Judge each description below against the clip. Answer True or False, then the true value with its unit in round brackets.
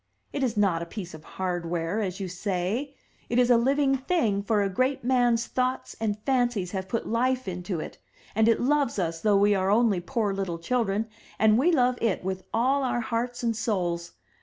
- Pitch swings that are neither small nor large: True (4.7 semitones)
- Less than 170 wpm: False (200 wpm)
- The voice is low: False (220 Hz)